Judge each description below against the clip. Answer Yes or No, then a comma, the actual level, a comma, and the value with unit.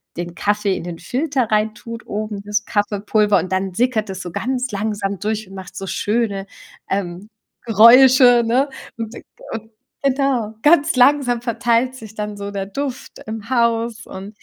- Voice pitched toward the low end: No, high, 220 Hz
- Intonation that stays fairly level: No, average, 3.3 semitones